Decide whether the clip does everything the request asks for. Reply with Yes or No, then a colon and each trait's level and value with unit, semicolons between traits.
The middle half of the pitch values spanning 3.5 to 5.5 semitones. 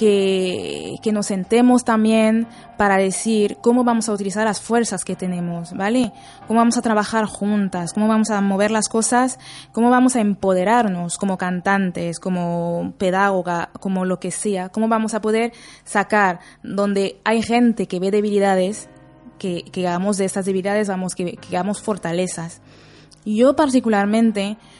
No: average, 3.1 semitones